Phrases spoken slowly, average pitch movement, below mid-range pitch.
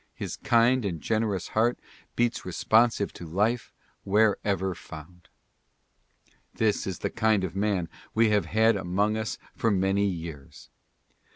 Yes: slow, 130 wpm; average, 3.3 semitones; low, 100 Hz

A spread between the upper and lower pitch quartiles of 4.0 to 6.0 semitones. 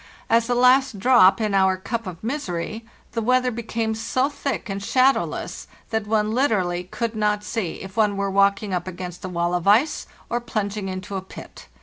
No: average, 3.6 semitones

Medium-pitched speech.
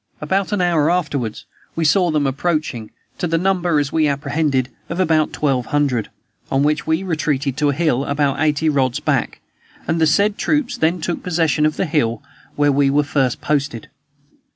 Yes: medium, 150 Hz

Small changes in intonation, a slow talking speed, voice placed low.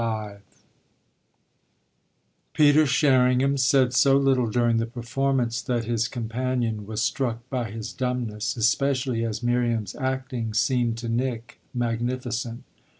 Yes: narrow, 2.1 semitones; slow, 115 wpm; low, 120 Hz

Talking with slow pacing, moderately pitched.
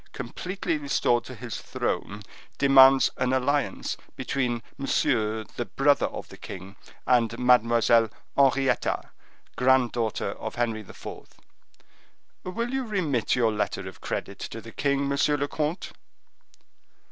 No: slow, 125 wpm; low, 130 Hz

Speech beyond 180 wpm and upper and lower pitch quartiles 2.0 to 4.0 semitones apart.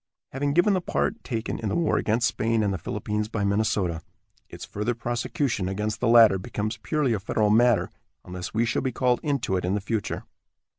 Yes: average, 200 wpm; average, 2.9 semitones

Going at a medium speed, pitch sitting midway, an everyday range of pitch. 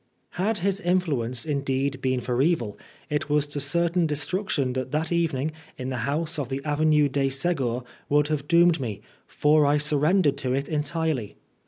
Yes: average, 180 wpm; medium, 145 Hz; average, 3.4 semitones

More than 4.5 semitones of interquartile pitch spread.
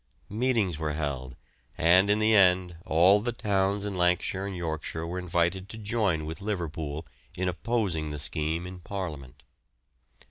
No: average, 4.0 semitones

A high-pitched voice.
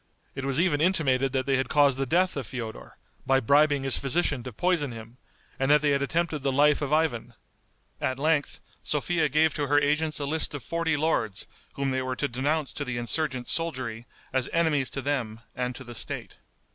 No: medium, 140 Hz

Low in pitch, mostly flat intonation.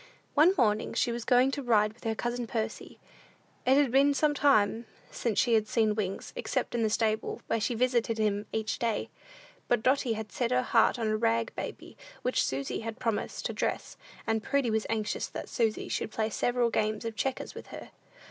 No: high, 230 Hz; narrow, 2.3 semitones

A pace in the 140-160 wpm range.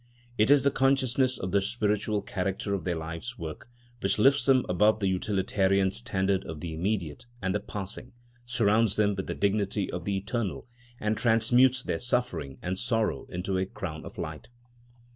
No: average, 175 wpm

